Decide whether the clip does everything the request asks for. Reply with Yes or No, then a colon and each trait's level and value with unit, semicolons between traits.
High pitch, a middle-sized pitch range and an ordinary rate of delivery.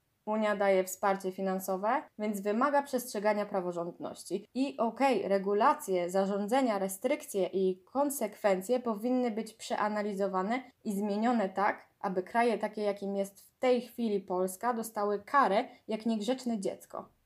Yes: high, 210 Hz; average, 3.4 semitones; average, 120 wpm